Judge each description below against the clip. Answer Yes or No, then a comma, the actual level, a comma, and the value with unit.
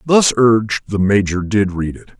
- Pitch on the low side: Yes, low, 105 Hz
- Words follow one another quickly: No, average, 190 wpm